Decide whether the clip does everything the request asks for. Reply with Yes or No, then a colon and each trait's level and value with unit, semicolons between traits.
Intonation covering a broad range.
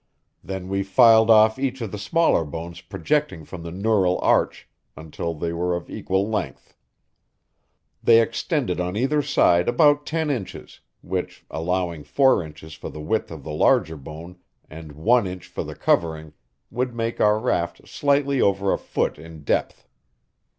Yes: wide, 5.9 semitones